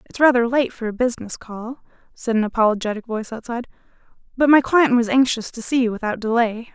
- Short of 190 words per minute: No, average, 195 wpm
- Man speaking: No, female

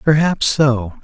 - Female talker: No, male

